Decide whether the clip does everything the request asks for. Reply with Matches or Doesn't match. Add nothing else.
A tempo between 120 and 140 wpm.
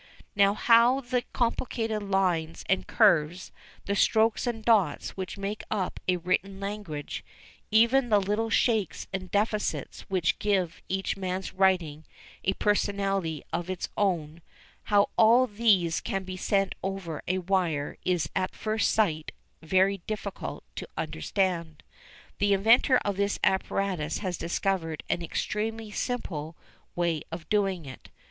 Matches